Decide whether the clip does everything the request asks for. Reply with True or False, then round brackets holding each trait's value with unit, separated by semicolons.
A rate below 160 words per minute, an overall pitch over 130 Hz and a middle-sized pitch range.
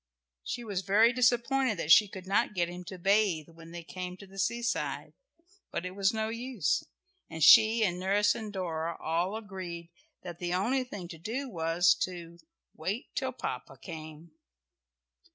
False (170 wpm; 185 Hz; 4.4 semitones)